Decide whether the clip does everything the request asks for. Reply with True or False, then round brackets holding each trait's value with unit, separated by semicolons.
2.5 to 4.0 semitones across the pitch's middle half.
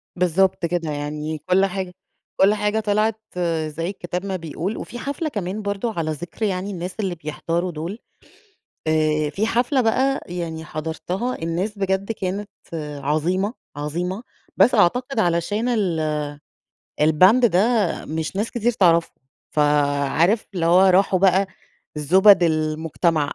False (4.4 semitones)